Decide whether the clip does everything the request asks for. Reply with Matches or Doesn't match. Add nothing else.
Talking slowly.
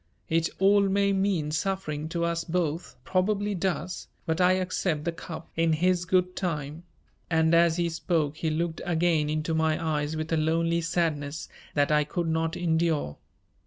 Doesn't match